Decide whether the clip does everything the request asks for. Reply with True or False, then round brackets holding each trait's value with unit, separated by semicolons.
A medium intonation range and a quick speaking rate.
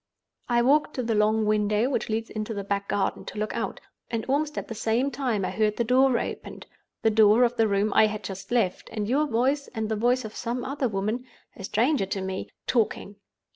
True (3.0 semitones; 215 wpm)